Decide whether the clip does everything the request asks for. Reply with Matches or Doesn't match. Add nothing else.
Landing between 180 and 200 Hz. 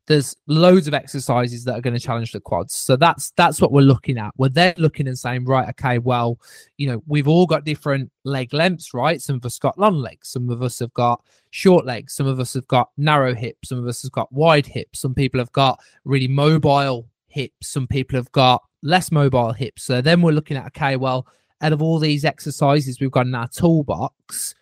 Doesn't match